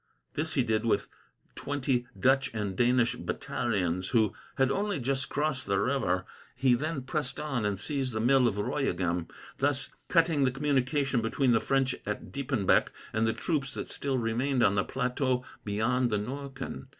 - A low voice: Yes, low, 125 Hz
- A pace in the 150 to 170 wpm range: Yes, average, 165 wpm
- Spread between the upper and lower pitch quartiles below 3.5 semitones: No, average, 3.8 semitones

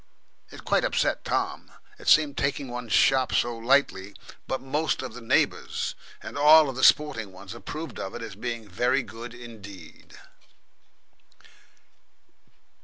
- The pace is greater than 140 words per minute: No, slow, 135 wpm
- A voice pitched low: Yes, low, 120 Hz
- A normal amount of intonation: Yes, average, 3.9 semitones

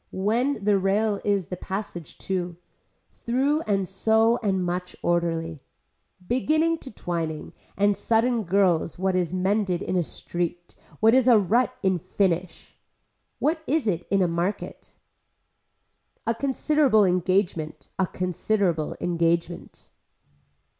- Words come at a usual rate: No, slow, 125 wpm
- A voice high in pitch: Yes, high, 195 Hz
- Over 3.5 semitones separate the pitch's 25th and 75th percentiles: Yes, average, 4.1 semitones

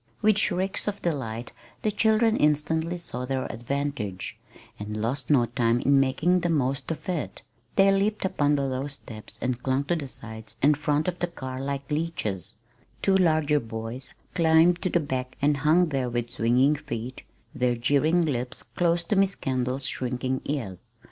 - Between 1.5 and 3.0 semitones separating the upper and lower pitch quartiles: No, average, 5.1 semitones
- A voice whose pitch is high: No, medium, 140 Hz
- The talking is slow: No, average, 170 wpm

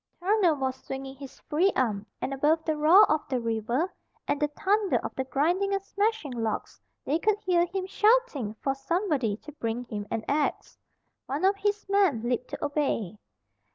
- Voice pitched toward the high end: Yes, very high, 295 Hz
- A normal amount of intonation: No, wide, 7.0 semitones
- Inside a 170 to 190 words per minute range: Yes, average, 180 wpm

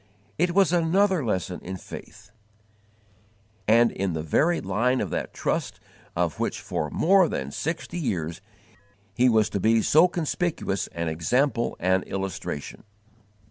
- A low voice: Yes, low, 115 Hz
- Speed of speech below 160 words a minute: Yes, average, 140 wpm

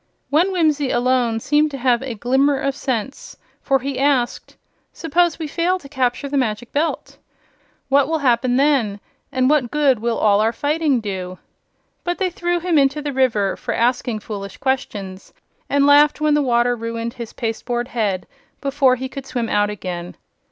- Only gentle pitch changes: No, average, 4.0 semitones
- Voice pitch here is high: Yes, very high, 260 Hz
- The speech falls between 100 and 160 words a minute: No, average, 175 wpm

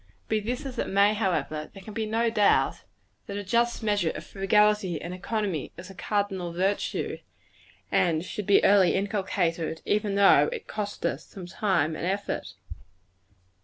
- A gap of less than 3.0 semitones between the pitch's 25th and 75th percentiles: Yes, narrow, 2.6 semitones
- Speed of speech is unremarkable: Yes, average, 165 wpm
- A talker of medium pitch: No, high, 200 Hz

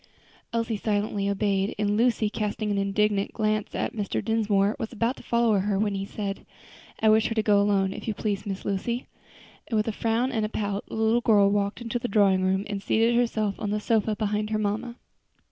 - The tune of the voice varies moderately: No, narrow, 1.8 semitones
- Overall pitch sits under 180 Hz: No, high, 210 Hz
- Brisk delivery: Yes, fast, 215 wpm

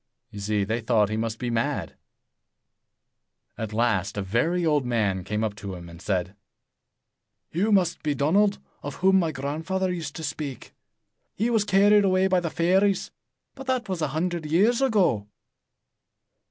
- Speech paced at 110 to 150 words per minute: No, average, 165 wpm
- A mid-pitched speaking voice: Yes, medium, 155 Hz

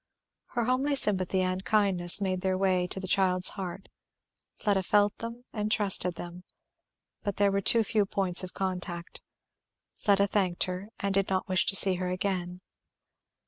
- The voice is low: No, high, 190 Hz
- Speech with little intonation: Yes, narrow, 1.8 semitones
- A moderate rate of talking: Yes, average, 165 wpm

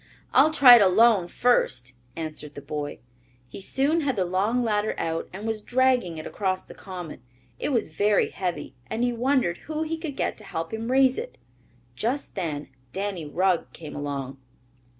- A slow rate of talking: No, average, 175 wpm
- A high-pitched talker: Yes, high, 200 Hz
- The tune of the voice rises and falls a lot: Yes, wide, 7.2 semitones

